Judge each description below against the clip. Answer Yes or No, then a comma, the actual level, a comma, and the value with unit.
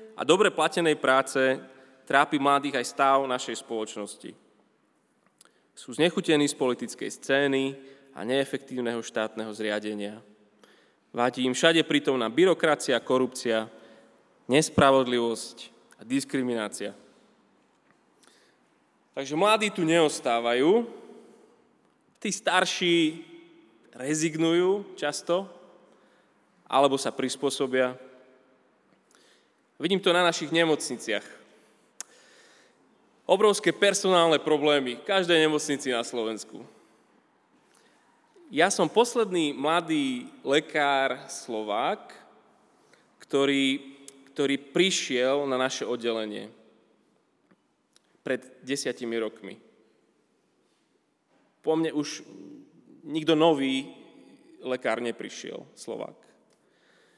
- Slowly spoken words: Yes, slow, 80 wpm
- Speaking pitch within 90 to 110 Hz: No, low, 135 Hz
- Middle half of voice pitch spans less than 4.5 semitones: No, average, 5.0 semitones